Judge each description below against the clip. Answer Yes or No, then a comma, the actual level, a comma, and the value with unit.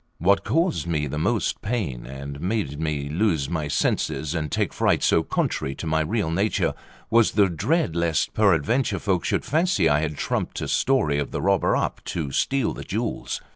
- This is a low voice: Yes, very low, 85 Hz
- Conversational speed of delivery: Yes, average, 185 wpm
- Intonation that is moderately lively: No, wide, 6.6 semitones